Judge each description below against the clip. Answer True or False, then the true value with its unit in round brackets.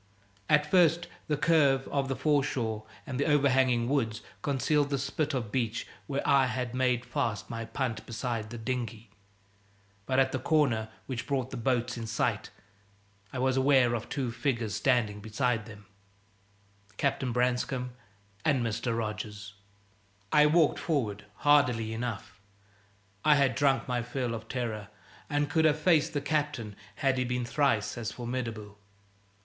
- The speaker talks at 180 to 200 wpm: False (150 wpm)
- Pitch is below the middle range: True (125 Hz)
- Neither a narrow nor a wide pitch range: True (3.6 semitones)